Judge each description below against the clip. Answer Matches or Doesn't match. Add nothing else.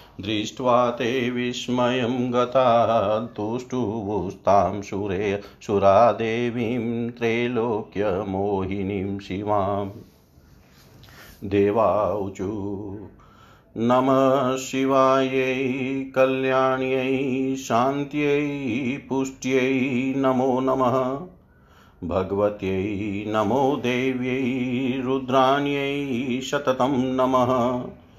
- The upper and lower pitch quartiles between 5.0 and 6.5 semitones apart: Doesn't match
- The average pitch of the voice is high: Doesn't match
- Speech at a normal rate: Doesn't match